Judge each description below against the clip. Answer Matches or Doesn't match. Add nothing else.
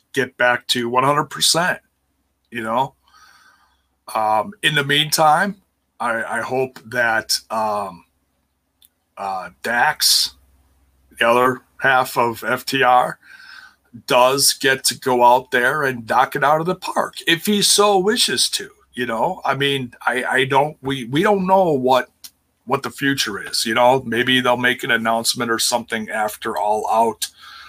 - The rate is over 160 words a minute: Doesn't match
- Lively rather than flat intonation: Doesn't match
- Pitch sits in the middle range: Doesn't match